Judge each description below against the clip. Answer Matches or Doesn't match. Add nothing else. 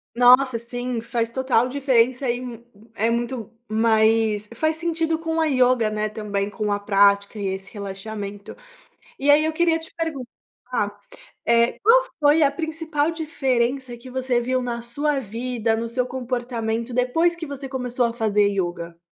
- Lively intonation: Doesn't match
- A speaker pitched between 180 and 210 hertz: Doesn't match